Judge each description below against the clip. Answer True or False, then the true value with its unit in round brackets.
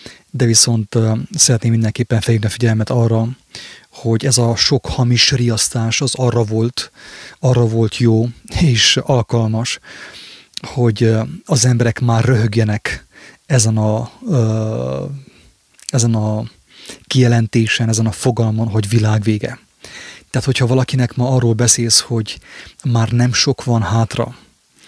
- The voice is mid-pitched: False (115 Hz)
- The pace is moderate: False (120 wpm)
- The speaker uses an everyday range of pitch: False (1.9 semitones)